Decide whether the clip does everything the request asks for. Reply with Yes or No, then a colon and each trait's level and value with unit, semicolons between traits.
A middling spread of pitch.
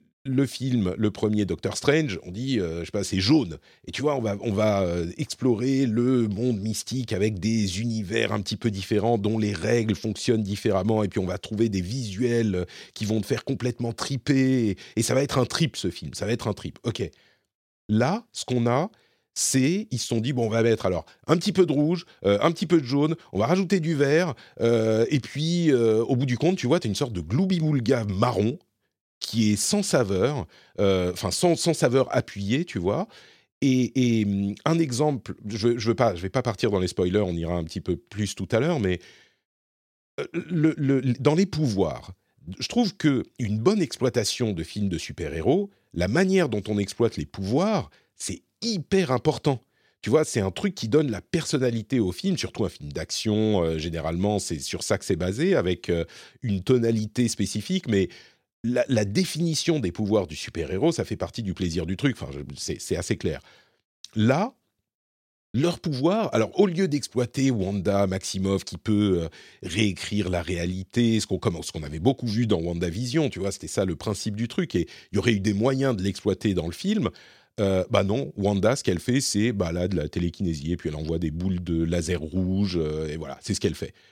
No: wide, 5.9 semitones